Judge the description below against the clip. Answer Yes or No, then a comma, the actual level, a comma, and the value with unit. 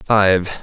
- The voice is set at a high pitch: No, low, 100 Hz